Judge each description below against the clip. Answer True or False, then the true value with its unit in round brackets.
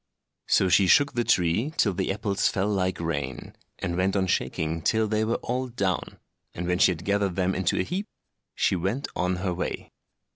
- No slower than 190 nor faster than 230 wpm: True (195 wpm)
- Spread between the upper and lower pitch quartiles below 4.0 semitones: True (3.1 semitones)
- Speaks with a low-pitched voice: True (95 Hz)